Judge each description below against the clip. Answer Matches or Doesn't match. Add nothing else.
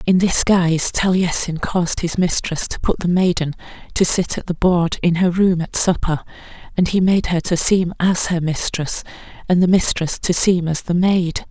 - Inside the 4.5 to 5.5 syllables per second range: Matches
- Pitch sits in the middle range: Matches